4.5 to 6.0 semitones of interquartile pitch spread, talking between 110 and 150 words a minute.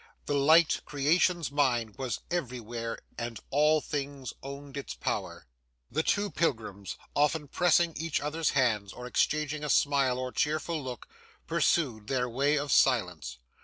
No: average, 3.7 semitones; average, 140 wpm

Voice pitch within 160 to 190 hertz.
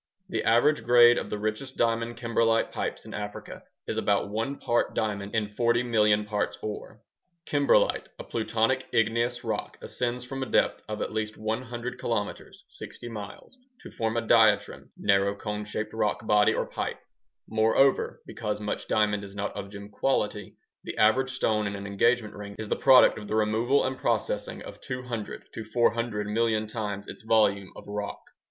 No: low, 110 Hz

